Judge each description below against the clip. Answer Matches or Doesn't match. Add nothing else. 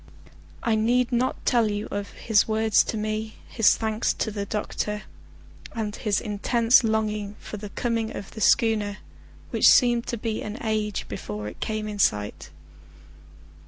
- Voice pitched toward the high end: Matches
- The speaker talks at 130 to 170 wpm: Matches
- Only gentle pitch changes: Matches